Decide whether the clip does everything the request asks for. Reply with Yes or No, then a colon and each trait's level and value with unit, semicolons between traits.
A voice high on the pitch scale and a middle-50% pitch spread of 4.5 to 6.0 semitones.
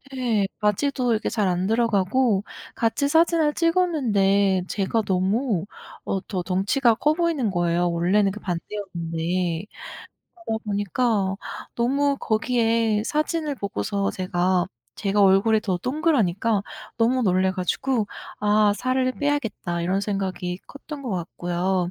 Yes: high, 210 Hz; average, 5.1 semitones